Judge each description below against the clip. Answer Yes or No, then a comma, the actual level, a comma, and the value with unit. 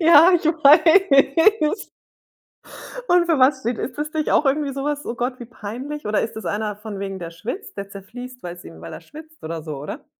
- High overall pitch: Yes, very high, 260 Hz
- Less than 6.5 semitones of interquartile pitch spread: No, wide, 6.9 semitones